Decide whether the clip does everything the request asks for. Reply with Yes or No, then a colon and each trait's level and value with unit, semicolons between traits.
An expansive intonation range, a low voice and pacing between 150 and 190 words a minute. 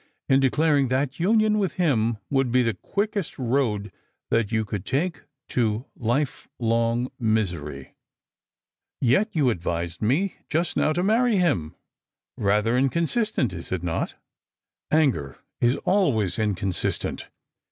No: wide, 7.1 semitones; low, 125 Hz; average, 140 wpm